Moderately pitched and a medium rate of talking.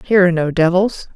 No: medium, 180 Hz; fast, 210 wpm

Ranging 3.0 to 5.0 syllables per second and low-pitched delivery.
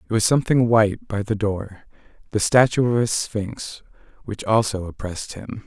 Yes: 4.9 syllables/s; low, 110 Hz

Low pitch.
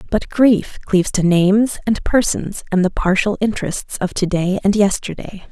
No: high, 200 Hz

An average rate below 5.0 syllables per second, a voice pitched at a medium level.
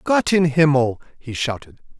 Yes: 4.5 syllables/s; medium, 145 Hz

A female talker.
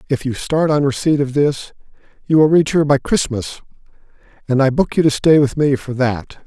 No: male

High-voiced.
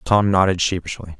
No: very low, 90 Hz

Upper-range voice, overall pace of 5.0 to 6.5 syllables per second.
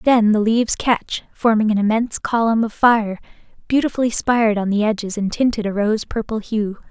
Yes: high, 220 Hz; 5.3 syllables/s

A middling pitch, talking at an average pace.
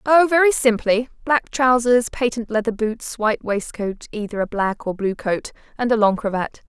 No: high, 230 Hz; average, 180 wpm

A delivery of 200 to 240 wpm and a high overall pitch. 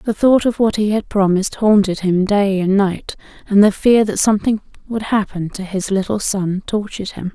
Yes: fast, 205 wpm; high, 200 Hz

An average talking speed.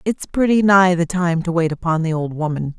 No: fast, 235 wpm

